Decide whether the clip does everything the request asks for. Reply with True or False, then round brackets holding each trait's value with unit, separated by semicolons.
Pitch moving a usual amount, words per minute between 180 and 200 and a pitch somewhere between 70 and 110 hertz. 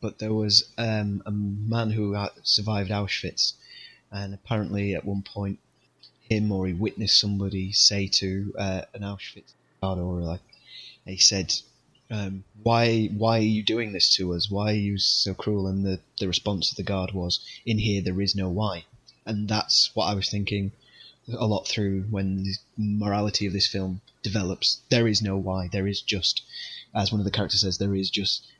False (1.8 semitones; 185 wpm; 100 Hz)